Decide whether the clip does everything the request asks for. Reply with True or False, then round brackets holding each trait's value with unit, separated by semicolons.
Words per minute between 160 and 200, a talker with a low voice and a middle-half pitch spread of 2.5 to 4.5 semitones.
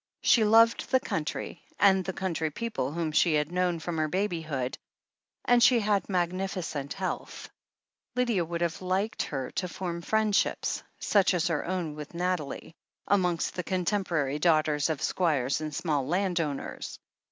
False (165 wpm; 175 Hz; 3.7 semitones)